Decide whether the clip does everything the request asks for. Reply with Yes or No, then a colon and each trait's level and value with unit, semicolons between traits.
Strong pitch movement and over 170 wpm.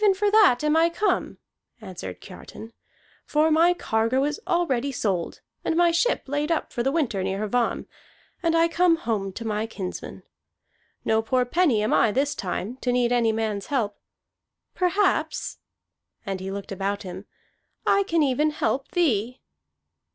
No: wide, 7.3 semitones; average, 160 wpm